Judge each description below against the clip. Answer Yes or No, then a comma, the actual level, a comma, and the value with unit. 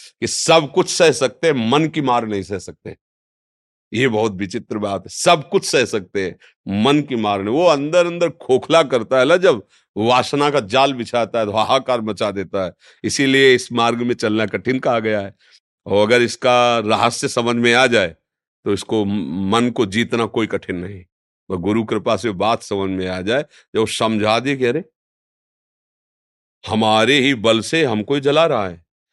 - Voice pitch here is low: Yes, low, 115 Hz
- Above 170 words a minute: Yes, average, 185 wpm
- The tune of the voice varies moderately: Yes, average, 4.2 semitones